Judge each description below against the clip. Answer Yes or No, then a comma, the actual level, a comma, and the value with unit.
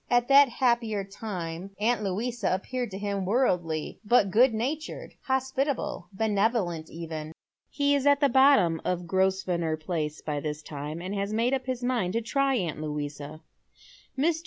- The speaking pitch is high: Yes, high, 200 Hz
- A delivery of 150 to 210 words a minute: Yes, average, 160 wpm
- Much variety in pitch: Yes, wide, 6.9 semitones